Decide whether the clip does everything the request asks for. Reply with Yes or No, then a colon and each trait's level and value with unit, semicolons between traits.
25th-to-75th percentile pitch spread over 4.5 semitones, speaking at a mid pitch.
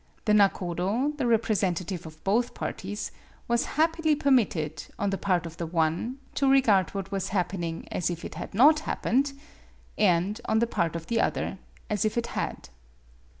No: average, 5.2 semitones; high, 200 Hz